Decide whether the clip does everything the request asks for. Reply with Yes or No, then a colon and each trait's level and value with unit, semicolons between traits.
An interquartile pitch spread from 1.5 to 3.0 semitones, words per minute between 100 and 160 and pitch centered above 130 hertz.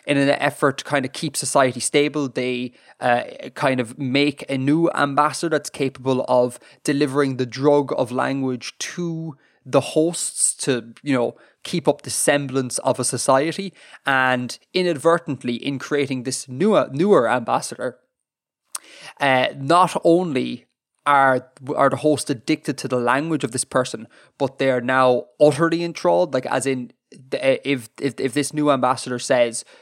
Yes: narrow, 2.4 semitones; average, 155 wpm; medium, 140 Hz